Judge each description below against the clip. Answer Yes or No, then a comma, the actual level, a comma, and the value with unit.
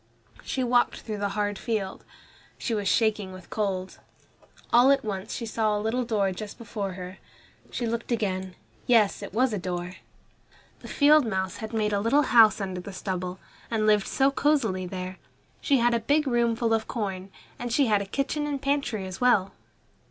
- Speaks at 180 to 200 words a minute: Yes, average, 190 wpm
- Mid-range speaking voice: No, high, 215 Hz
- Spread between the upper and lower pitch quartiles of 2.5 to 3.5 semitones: No, average, 3.9 semitones